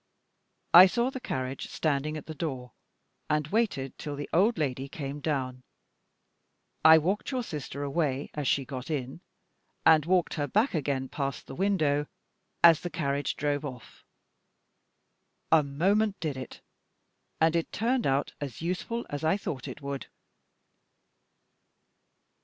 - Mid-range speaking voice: Yes, medium, 150 Hz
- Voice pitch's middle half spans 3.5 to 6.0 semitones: Yes, average, 3.9 semitones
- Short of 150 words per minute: Yes, average, 140 wpm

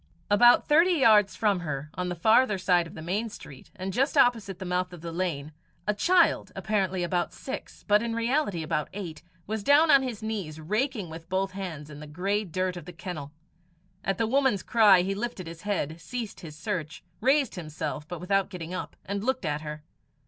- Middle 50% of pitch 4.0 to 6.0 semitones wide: Yes, average, 4.8 semitones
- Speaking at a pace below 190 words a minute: No, average, 200 wpm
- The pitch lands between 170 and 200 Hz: Yes, high, 190 Hz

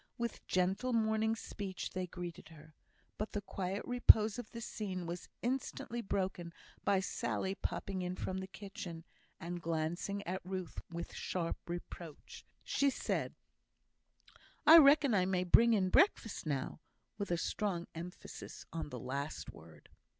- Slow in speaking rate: No, average, 145 wpm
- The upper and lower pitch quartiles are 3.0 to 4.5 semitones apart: Yes, average, 3.9 semitones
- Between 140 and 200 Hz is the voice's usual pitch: Yes, high, 190 Hz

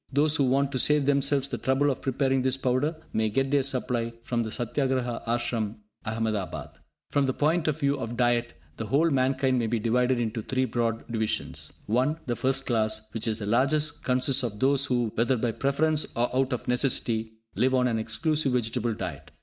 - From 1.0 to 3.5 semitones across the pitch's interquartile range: Yes, average, 3.0 semitones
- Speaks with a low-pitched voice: Yes, low, 125 Hz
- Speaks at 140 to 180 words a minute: No, average, 195 wpm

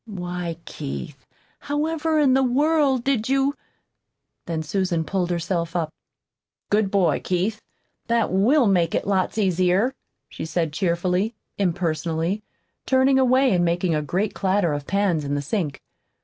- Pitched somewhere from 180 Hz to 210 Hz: Yes, high, 190 Hz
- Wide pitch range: Yes, wide, 6.2 semitones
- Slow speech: No, average, 145 wpm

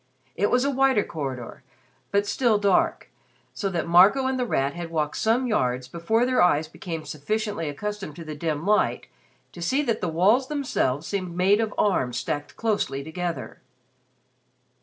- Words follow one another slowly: No, average, 165 wpm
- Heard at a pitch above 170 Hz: Yes, medium, 185 Hz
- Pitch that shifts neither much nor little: No, wide, 6.1 semitones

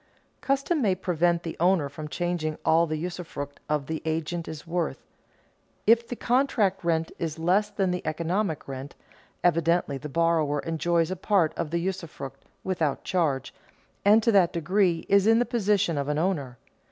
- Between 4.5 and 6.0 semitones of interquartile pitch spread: No, average, 3.4 semitones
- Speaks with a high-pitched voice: No, medium, 170 Hz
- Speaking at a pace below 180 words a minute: Yes, average, 165 wpm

